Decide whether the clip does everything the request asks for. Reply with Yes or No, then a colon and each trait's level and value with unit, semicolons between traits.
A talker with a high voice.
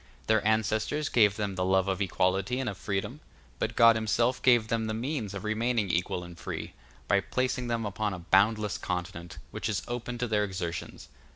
No: low, 105 Hz